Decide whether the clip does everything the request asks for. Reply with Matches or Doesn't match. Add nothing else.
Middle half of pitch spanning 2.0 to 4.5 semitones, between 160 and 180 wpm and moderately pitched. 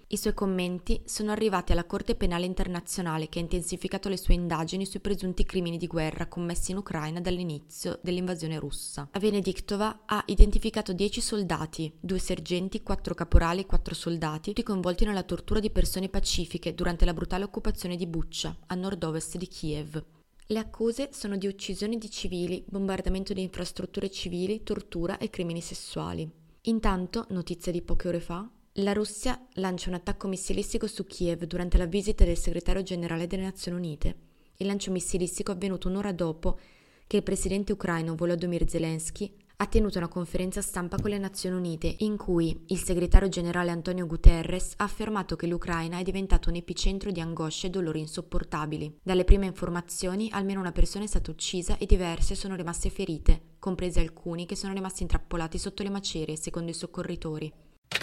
Matches